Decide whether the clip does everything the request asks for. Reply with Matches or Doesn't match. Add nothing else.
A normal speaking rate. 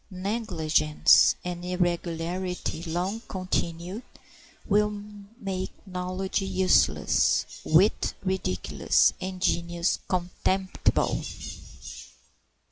Doesn't match